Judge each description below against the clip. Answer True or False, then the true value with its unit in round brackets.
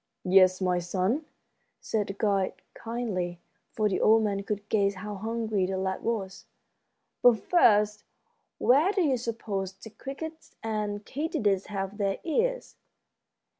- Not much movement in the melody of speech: False (3.2 semitones)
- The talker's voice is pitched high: True (210 Hz)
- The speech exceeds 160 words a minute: False (135 wpm)